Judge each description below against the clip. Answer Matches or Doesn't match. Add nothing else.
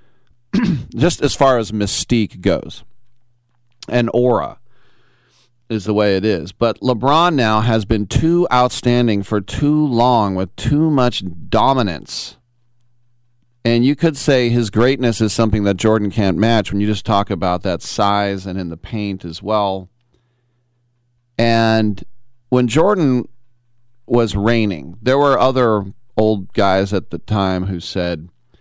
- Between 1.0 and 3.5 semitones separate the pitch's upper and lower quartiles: Matches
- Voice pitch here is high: Doesn't match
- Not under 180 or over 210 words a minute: Doesn't match